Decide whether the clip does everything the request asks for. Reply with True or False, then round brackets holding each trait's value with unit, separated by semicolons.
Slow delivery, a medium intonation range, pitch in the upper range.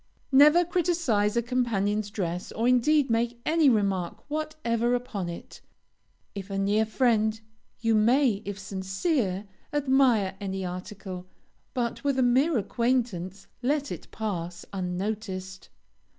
True (120 wpm; 4.9 semitones; 220 Hz)